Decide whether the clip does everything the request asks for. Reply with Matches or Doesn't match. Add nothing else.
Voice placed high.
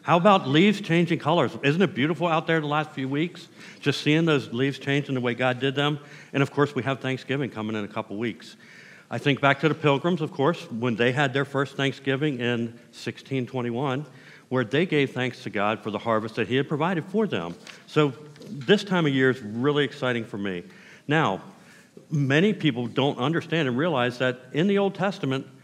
Doesn't match